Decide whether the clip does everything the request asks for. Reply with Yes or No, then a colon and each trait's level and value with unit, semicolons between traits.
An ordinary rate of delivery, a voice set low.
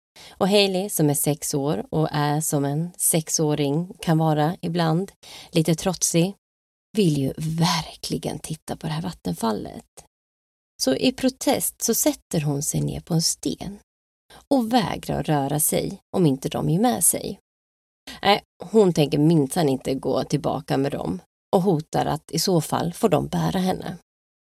No: average, 155 wpm; medium, 160 Hz